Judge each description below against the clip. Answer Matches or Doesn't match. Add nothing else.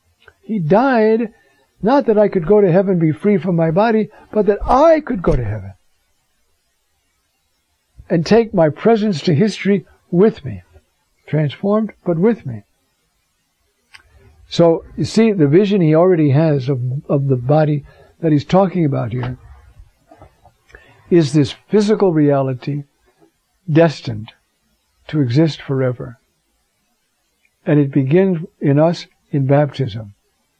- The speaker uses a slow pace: Matches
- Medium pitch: Matches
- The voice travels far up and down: Matches